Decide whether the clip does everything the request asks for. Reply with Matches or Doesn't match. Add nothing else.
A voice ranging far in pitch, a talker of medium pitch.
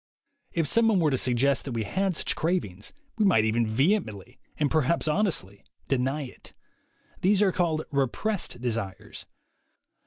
Matches